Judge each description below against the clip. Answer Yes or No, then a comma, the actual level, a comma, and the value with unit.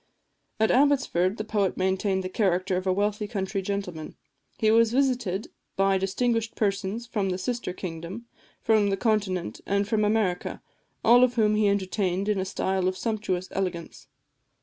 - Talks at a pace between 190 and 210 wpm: No, average, 160 wpm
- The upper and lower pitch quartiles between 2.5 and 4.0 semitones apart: Yes, average, 2.8 semitones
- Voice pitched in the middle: No, high, 200 Hz